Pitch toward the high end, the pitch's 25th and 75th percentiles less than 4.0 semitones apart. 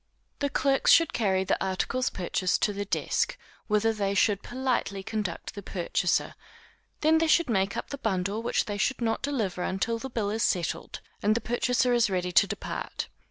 No: high, 215 Hz; average, 4.4 semitones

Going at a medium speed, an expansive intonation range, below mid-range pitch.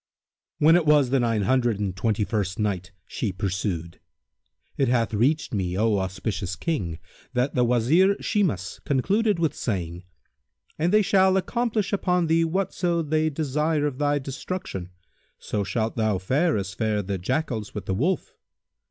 Yes: average, 155 wpm; wide, 8.2 semitones; low, 125 Hz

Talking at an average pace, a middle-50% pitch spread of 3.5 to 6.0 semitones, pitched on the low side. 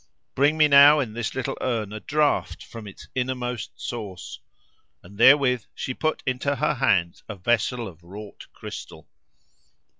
Yes: average, 150 wpm; average, 4.8 semitones; low, 125 Hz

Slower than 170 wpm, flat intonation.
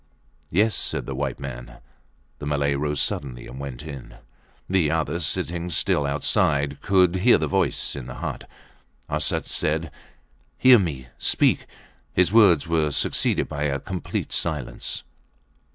No: average, 140 wpm; average, 4.0 semitones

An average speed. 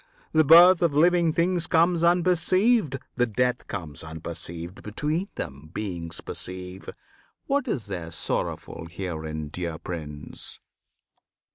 No: slow, 115 wpm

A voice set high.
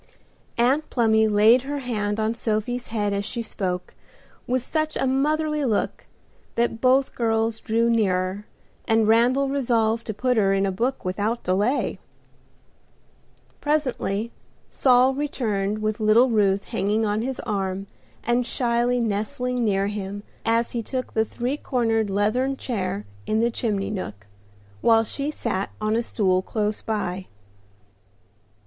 Yes: high, 225 Hz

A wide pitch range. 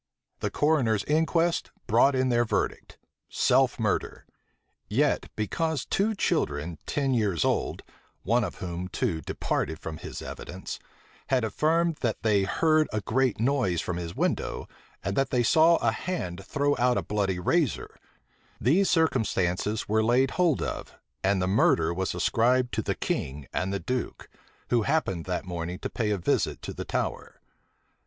Yes: wide, 7.3 semitones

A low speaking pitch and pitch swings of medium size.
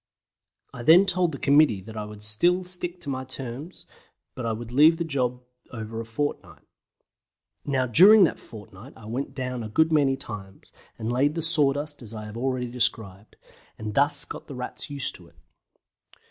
Yes: low, 130 Hz; average, 5.0 semitones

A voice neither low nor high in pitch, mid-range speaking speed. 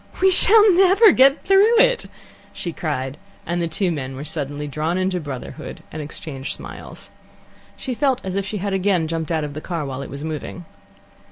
Yes: medium, 170 Hz; average, 190 wpm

